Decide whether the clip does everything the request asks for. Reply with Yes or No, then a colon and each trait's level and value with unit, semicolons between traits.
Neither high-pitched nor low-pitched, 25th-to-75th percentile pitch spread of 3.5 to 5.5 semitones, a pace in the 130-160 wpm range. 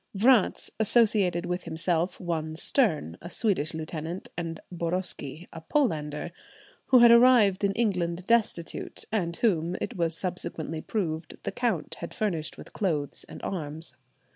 Yes: medium, 175 Hz; average, 4.4 semitones; average, 140 wpm